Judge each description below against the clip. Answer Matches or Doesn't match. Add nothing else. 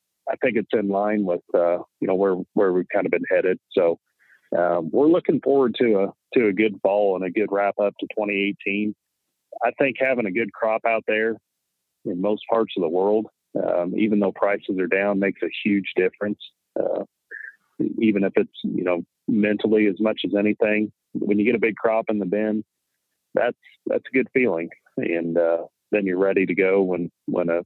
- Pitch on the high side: Doesn't match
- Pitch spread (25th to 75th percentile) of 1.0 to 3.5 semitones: Matches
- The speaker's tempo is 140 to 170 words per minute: Doesn't match